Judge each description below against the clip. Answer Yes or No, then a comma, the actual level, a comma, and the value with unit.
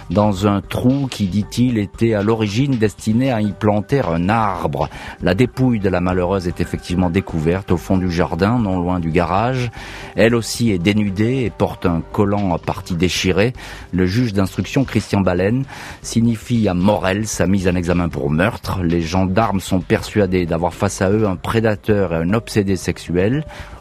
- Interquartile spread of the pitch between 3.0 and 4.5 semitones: Yes, average, 3.8 semitones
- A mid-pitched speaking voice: No, low, 100 Hz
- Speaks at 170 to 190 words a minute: Yes, average, 175 wpm